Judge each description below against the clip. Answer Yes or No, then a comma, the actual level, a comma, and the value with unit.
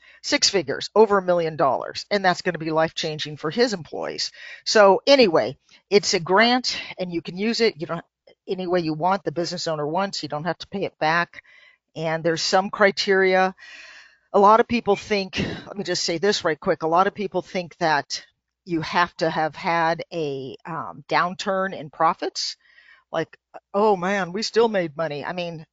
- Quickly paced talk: No, average, 195 wpm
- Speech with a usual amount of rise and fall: Yes, average, 3.5 semitones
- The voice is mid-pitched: Yes, medium, 180 Hz